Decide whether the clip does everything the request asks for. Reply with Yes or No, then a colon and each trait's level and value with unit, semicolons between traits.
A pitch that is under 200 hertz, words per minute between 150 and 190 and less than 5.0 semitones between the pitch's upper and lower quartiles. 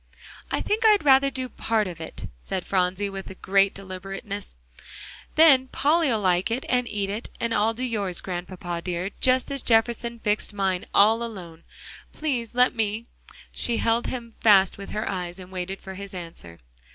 No: high, 205 Hz; average, 170 wpm; average, 4.0 semitones